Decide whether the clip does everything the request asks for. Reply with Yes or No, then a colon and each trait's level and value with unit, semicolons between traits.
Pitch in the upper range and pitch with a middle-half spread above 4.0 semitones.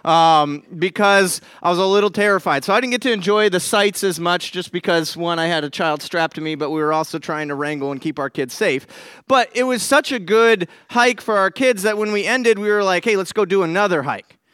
Yes: high, 195 Hz; average, 4.8 semitones